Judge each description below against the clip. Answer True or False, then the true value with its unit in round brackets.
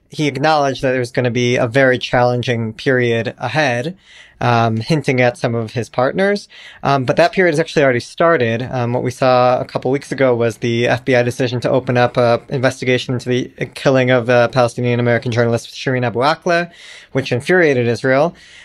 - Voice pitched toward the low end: True (125 Hz)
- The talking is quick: False (185 wpm)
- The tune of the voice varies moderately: False (2.3 semitones)